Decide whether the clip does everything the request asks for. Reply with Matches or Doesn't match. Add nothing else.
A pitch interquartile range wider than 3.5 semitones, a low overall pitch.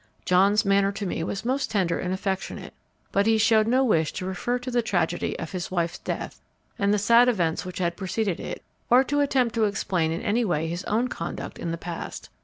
Doesn't match